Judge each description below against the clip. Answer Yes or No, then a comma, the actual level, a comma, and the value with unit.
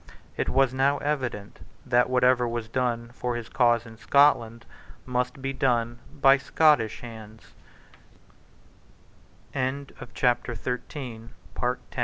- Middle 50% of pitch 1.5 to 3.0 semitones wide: Yes, narrow, 2.4 semitones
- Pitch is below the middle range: Yes, low, 125 Hz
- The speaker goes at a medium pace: No, slow, 105 wpm